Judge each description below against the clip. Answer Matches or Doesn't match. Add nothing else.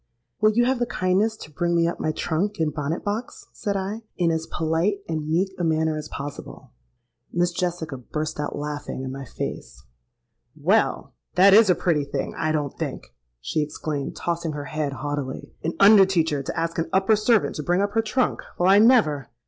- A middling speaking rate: Matches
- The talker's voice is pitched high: Doesn't match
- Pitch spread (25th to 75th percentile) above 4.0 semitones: Matches